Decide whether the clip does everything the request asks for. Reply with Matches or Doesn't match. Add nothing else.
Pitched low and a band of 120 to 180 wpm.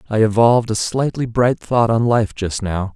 Doesn't match